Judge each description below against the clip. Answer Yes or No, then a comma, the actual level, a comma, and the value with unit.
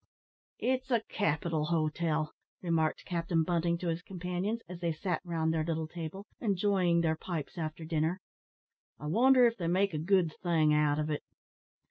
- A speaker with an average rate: Yes, average, 165 wpm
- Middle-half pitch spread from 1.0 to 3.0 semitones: Yes, average, 2.7 semitones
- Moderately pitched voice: Yes, medium, 170 Hz